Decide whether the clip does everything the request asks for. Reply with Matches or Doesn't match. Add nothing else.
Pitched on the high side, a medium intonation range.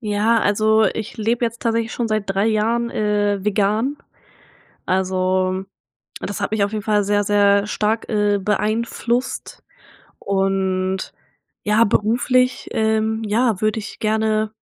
Doesn't match